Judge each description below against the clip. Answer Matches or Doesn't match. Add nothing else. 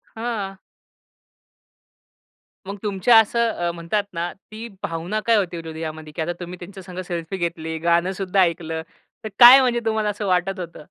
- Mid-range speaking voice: Matches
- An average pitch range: Matches